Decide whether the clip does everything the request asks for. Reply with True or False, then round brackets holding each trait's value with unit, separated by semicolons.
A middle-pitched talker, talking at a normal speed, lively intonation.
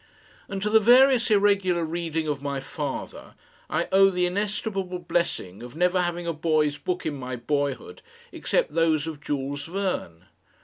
False (170 Hz; 160 wpm; 4.9 semitones)